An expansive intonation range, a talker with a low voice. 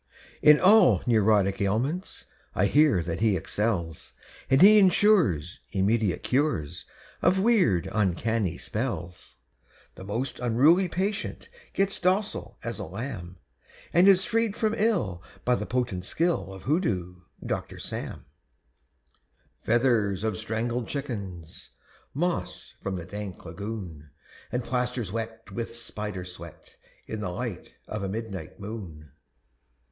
Yes: wide, 7.1 semitones; low, 110 Hz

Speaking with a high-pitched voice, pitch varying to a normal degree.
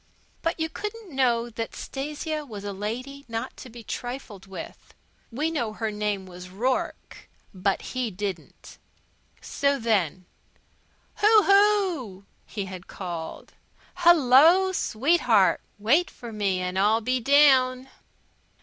No: high, 240 Hz; wide, 6.4 semitones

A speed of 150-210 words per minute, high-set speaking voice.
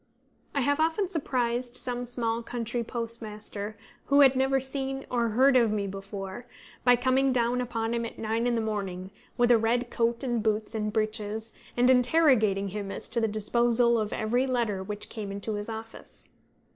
Yes: average, 180 wpm; high, 235 Hz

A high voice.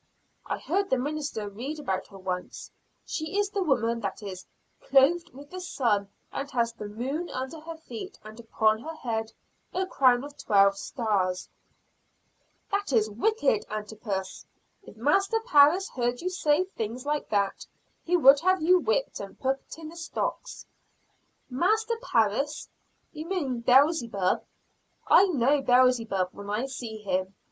Yes: very high, 260 Hz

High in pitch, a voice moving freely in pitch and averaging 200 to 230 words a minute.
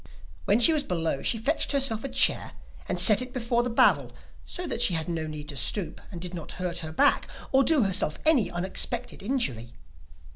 Yes: high, 200 Hz; wide, 7.3 semitones; fast, 205 wpm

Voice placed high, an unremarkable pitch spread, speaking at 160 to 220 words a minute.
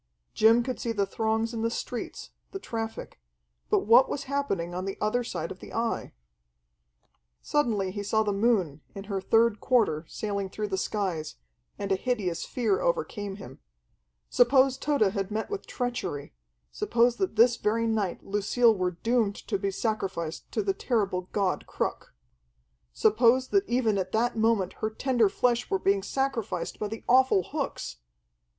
Yes: high, 220 Hz; average, 3.6 semitones; average, 165 wpm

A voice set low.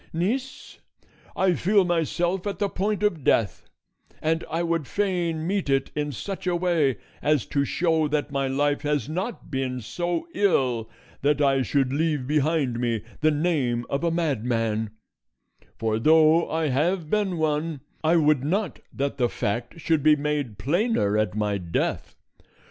No: medium, 150 Hz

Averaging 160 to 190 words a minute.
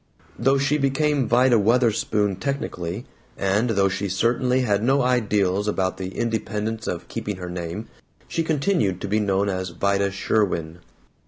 No: average, 150 wpm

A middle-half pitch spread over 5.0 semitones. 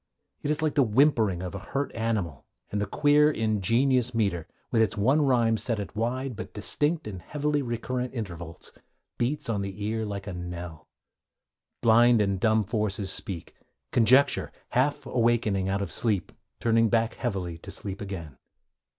No: average, 4.3 semitones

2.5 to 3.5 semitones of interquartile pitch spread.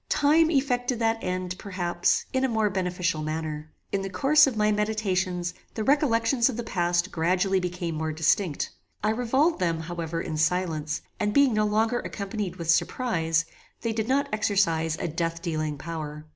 No: average, 5.3 semitones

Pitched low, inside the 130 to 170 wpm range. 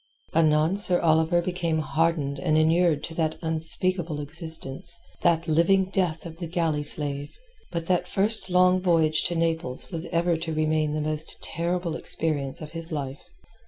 No: medium, 165 Hz; average, 160 wpm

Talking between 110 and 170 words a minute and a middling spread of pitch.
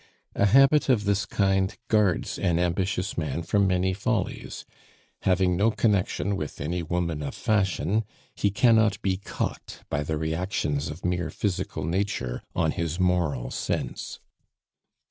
Yes: average, 140 wpm; average, 3.6 semitones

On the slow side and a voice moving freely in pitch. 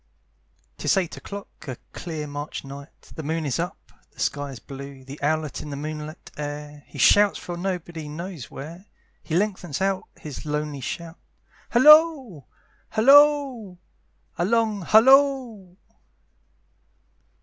Yes: slow, 130 wpm; wide, 6.0 semitones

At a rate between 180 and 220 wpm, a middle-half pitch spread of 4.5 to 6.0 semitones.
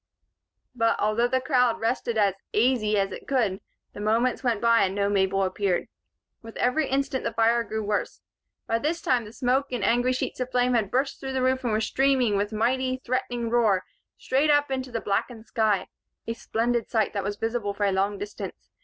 No: fast, 205 wpm; average, 3.5 semitones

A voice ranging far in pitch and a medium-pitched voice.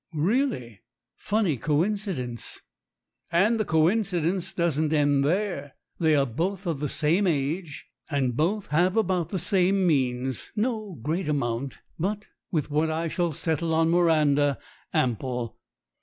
No: average, 4.8 semitones; medium, 160 Hz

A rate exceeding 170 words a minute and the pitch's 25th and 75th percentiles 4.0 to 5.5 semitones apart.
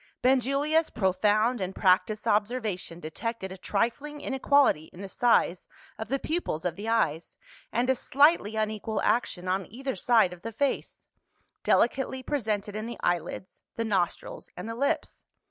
No: average, 150 wpm; average, 5.2 semitones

